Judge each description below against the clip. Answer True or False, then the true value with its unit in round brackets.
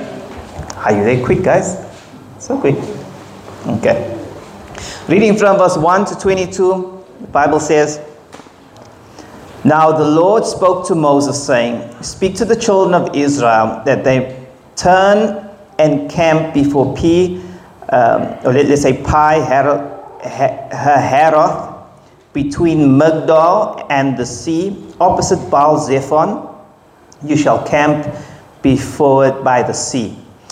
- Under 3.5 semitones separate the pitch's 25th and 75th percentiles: False (4.4 semitones)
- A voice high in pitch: False (150 Hz)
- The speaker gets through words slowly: True (120 wpm)